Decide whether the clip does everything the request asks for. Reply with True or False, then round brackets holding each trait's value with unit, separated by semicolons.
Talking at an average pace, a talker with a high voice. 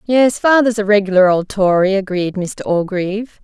True (155 wpm; 200 Hz)